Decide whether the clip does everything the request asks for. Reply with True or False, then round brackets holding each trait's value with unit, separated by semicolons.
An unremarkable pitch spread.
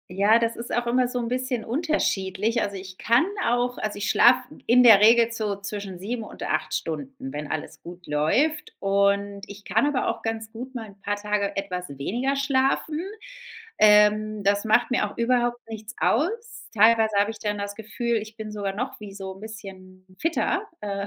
True (3.3 semitones)